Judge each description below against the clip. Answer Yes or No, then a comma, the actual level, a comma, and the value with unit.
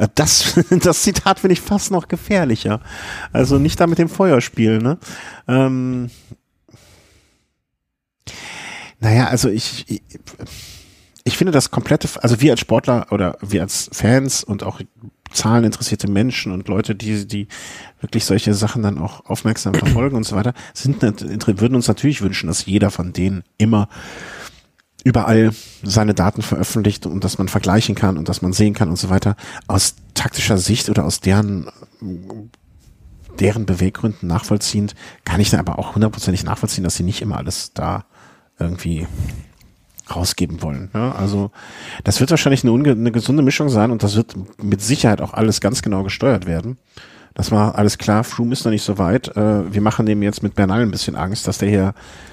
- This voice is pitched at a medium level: No, low, 105 Hz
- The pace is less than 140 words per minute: No, average, 165 wpm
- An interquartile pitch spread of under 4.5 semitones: Yes, average, 3.8 semitones